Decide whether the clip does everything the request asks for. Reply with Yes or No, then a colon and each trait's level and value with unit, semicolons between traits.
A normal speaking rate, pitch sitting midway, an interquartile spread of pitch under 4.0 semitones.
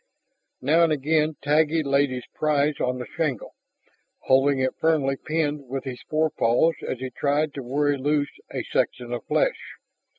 Yes: average, 160 wpm; medium, 145 Hz; average, 2.7 semitones